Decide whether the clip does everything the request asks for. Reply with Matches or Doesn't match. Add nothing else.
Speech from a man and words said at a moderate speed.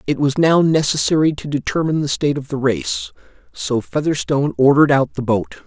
Matches